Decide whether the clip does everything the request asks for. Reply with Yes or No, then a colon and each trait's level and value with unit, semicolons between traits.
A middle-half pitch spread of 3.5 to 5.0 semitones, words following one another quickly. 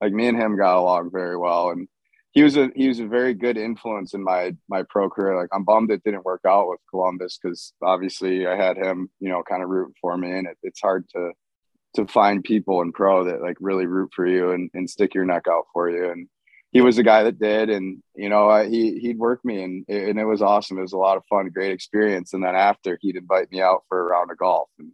No: average, 2.9 semitones; fast, 260 wpm